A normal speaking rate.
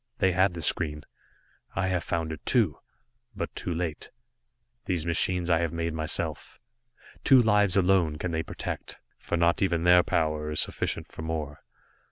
Yes: average, 165 wpm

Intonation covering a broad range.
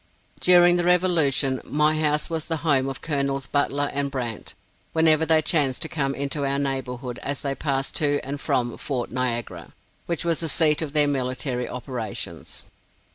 No: average, 2.9 semitones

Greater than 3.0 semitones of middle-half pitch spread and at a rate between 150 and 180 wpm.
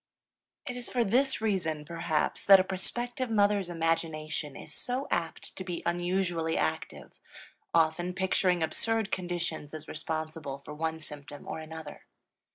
No: average, 3.6 semitones; average, 140 wpm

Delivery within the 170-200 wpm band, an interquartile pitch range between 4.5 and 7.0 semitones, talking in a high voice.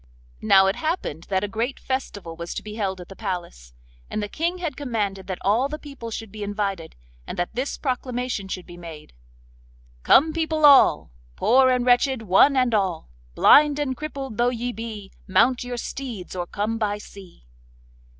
Yes: average, 180 wpm; wide, 5.4 semitones; high, 225 Hz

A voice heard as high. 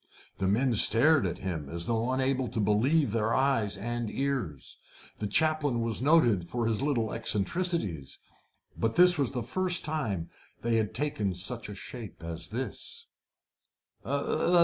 No: low, 115 Hz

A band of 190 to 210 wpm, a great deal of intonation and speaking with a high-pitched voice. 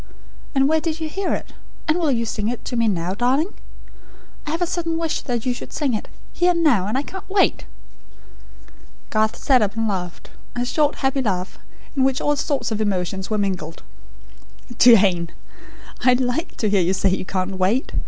Yes: average, 195 wpm; wide, 6.9 semitones; high, 245 Hz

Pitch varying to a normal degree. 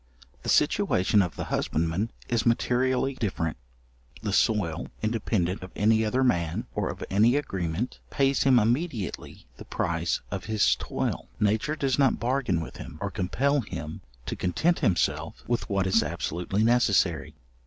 No: wide, 5.7 semitones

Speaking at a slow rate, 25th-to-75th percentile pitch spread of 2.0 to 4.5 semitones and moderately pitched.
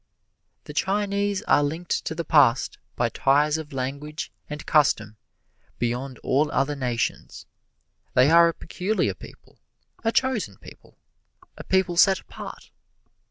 No: slow, 130 wpm; average, 5.1 semitones; medium, 150 Hz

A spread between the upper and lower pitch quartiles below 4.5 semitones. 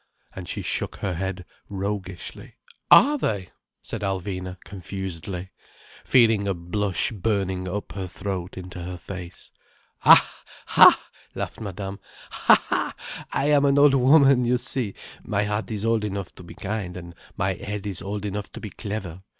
Yes: average, 2.7 semitones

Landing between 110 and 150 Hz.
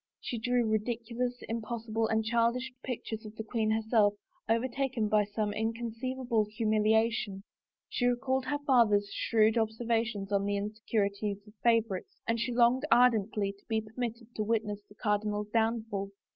No: high, 225 Hz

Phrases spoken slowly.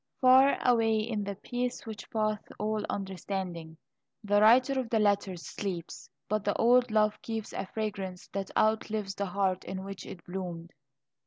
No: average, 160 wpm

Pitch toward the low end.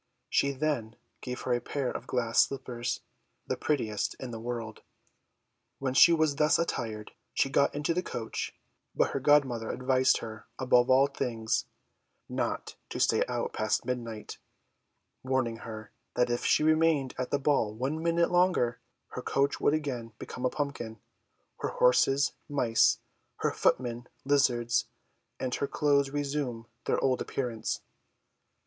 Yes: low, 130 Hz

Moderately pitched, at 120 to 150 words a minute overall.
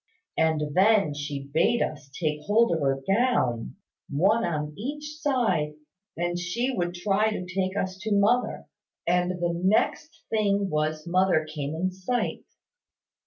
Yes: medium, 180 Hz; average, 145 wpm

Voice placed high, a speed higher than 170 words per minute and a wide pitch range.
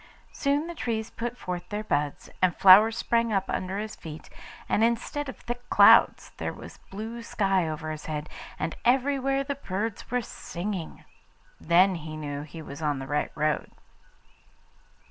No: high, 195 Hz; average, 165 wpm; wide, 7.0 semitones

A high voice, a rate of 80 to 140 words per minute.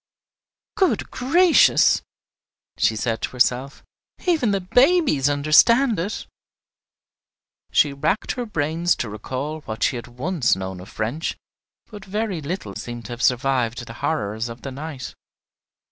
No: medium, 145 Hz; slow, 135 wpm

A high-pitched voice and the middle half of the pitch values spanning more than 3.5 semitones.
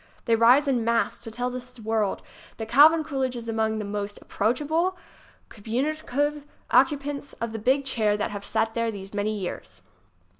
Yes: high, 235 Hz; average, 4.2 semitones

